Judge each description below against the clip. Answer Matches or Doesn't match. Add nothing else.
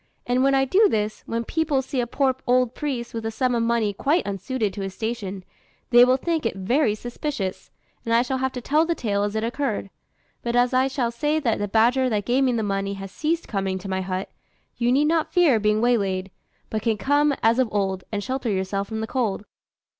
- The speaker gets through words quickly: Matches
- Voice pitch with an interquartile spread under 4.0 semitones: Doesn't match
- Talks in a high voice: Matches